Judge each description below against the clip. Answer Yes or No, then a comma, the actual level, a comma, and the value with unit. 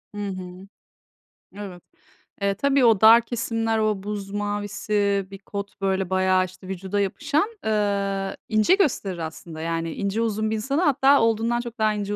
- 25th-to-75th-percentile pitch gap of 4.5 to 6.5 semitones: No, average, 2.8 semitones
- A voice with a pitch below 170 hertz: No, high, 205 Hz